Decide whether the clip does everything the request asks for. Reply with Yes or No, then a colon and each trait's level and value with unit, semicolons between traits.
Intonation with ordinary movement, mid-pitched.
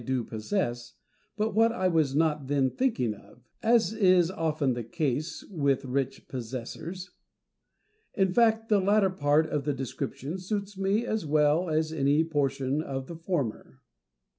No: wide, 6.0 semitones; medium, 155 Hz